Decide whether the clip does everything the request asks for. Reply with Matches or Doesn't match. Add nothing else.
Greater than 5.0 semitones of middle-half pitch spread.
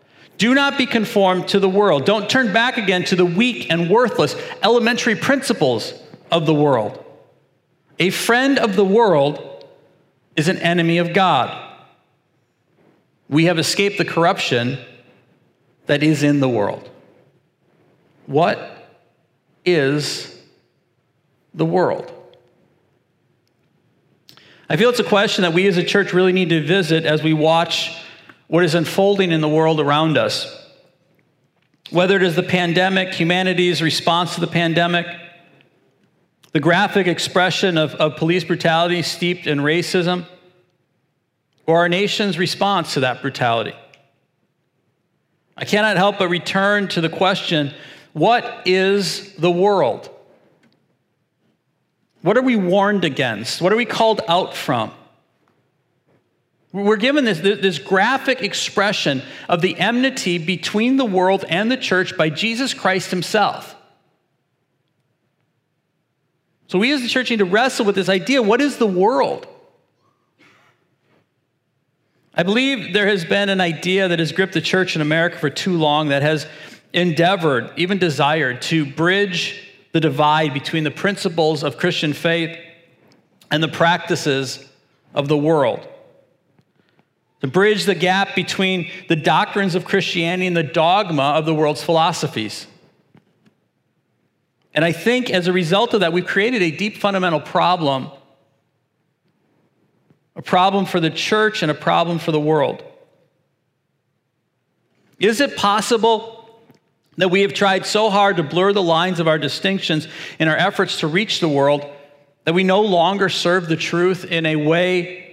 Doesn't match